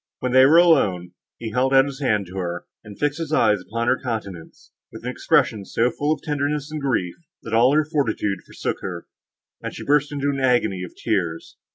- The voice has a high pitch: No, low, 125 Hz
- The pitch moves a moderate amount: No, wide, 6.5 semitones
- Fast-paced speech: Yes, fast, 210 wpm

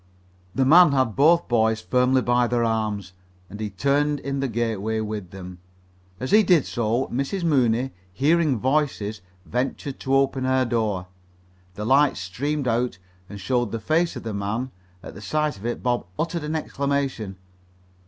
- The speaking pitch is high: No, low, 125 Hz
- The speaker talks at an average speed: Yes, average, 165 wpm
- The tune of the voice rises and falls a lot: No, average, 4.3 semitones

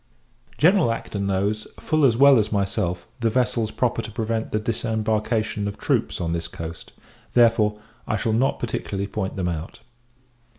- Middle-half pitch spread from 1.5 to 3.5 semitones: Yes, average, 2.8 semitones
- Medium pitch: No, low, 110 Hz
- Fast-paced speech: No, average, 160 wpm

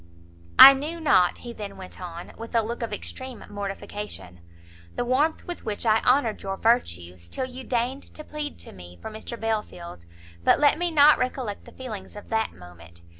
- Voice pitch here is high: Yes, high, 220 Hz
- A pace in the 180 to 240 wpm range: Yes, average, 185 wpm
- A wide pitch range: Yes, wide, 5.7 semitones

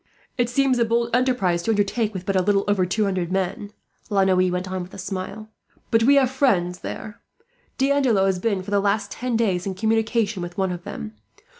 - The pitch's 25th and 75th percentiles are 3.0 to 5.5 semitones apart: Yes, average, 3.7 semitones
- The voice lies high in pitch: Yes, high, 205 Hz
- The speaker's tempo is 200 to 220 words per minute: Yes, fast, 205 wpm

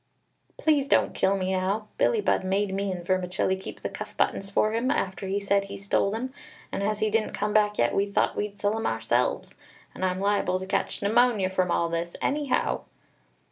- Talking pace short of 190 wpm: No, fast, 205 wpm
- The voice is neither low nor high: No, high, 200 Hz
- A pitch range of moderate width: No, narrow, 2.3 semitones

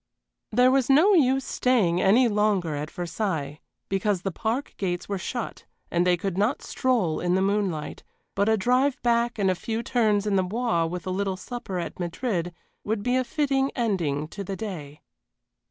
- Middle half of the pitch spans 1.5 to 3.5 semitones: No, average, 5.2 semitones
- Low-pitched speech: No, high, 200 Hz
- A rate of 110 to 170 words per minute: No, average, 185 wpm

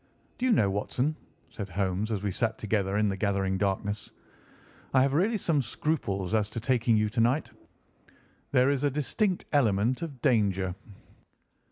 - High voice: No, low, 110 Hz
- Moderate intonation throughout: No, wide, 5.7 semitones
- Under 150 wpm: No, average, 165 wpm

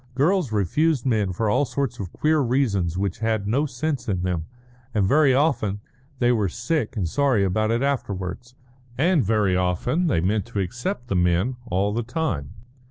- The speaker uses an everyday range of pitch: No, wide, 6.1 semitones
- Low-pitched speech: Yes, low, 115 Hz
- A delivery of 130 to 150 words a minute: No, average, 175 wpm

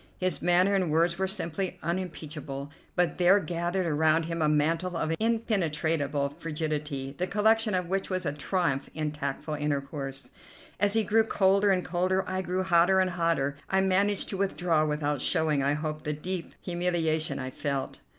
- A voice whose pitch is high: No, medium, 170 Hz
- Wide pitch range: No, average, 3.8 semitones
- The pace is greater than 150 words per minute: Yes, average, 170 wpm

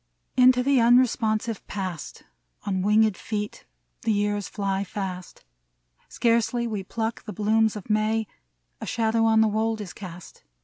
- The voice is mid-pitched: No, high, 215 Hz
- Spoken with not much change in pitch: Yes, narrow, 1.9 semitones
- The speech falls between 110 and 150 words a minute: Yes, average, 140 wpm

